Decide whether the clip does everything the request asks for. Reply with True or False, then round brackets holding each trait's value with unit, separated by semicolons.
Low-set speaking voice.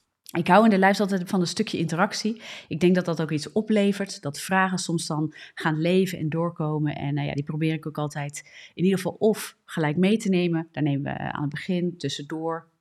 False (165 Hz)